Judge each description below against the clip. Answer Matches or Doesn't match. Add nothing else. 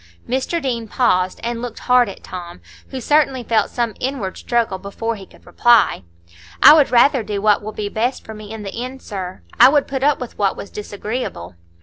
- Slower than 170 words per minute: Doesn't match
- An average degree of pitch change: Matches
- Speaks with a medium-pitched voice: Doesn't match